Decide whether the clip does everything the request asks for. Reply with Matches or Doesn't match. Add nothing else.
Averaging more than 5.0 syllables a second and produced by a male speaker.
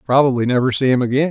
Matches